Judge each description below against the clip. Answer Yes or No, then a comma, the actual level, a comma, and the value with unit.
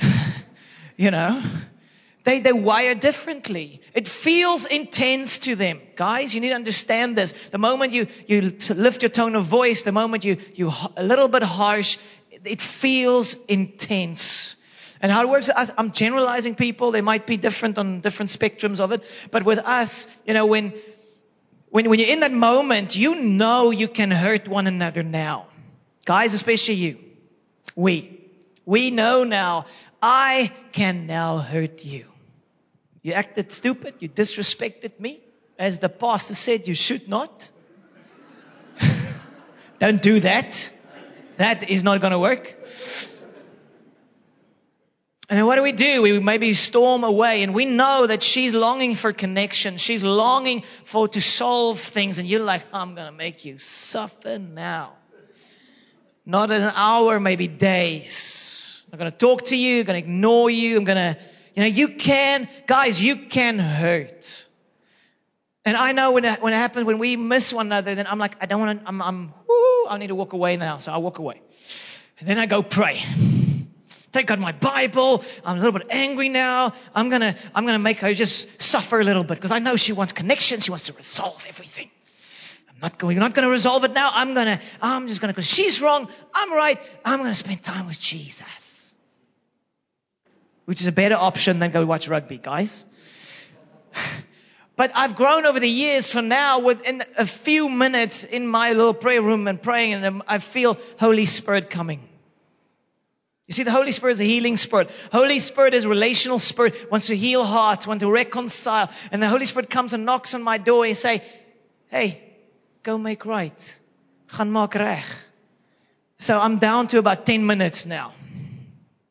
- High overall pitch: Yes, high, 220 Hz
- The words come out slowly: No, average, 175 wpm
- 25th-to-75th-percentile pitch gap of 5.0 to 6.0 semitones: No, average, 4.0 semitones